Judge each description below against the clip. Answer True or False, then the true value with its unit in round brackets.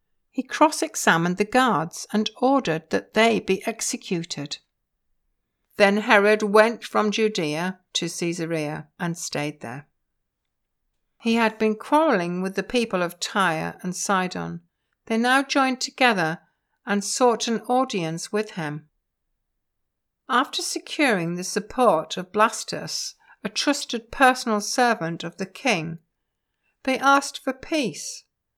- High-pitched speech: True (210 Hz)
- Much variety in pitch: True (6.6 semitones)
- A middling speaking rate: False (125 wpm)